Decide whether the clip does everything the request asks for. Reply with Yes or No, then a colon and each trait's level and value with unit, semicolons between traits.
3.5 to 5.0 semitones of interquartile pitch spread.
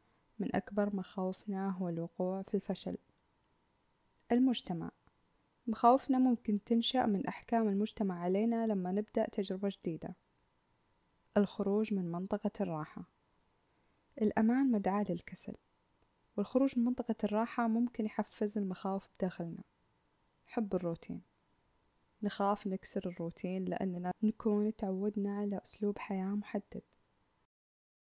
No: average, 3.0 semitones